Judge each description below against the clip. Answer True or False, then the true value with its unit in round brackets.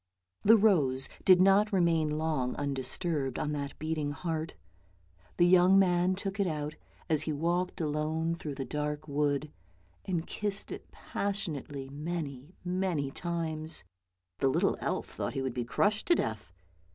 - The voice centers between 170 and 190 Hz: False (160 Hz)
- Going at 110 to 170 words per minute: True (150 wpm)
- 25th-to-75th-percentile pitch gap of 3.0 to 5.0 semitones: True (3.9 semitones)